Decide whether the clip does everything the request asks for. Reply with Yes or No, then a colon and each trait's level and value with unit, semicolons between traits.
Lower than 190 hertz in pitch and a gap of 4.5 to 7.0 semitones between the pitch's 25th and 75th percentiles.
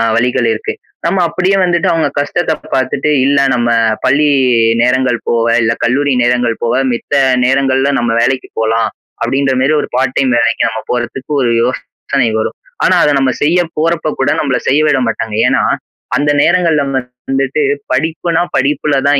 No: low, 135 Hz; average, 3.7 semitones